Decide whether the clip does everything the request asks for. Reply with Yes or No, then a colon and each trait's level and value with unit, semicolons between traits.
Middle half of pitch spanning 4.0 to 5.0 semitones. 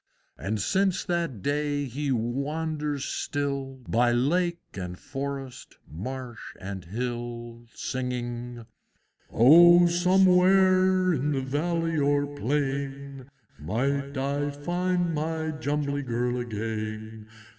Yes: average, 4.7 semitones